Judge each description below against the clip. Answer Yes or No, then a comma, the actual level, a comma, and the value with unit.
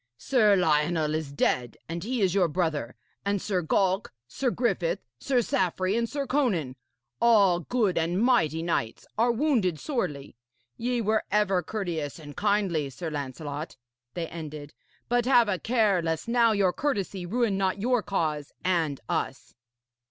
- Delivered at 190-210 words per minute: No, average, 150 wpm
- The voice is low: No, medium, 185 Hz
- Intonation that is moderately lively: No, wide, 6.1 semitones